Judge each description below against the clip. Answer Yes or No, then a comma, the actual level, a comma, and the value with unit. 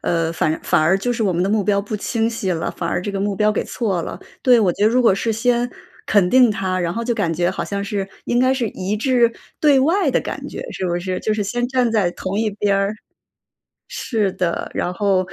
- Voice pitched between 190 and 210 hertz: Yes, high, 205 Hz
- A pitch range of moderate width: Yes, average, 4.0 semitones